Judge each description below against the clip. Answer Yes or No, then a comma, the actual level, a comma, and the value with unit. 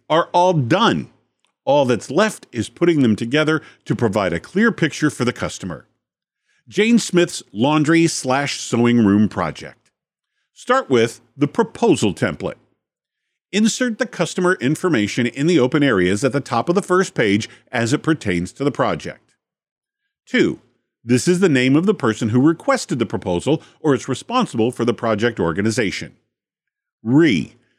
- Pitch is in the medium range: Yes, medium, 145 Hz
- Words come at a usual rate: Yes, average, 155 wpm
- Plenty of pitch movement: Yes, wide, 7.4 semitones